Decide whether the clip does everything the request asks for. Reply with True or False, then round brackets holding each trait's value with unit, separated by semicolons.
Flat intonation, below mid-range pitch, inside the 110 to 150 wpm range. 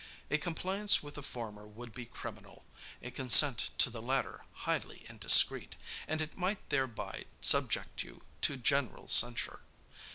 False (4.7 semitones; 130 Hz; 140 wpm)